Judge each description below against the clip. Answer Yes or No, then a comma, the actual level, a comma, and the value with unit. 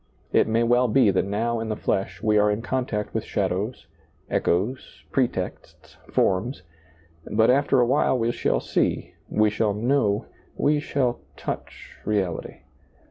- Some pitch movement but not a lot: Yes, average, 3.3 semitones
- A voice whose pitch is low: Yes, low, 110 Hz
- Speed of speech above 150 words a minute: No, average, 140 wpm